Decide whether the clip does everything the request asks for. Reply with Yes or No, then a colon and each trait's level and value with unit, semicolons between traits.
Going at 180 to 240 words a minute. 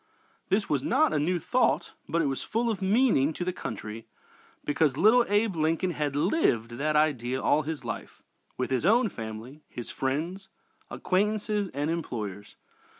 No: average, 160 wpm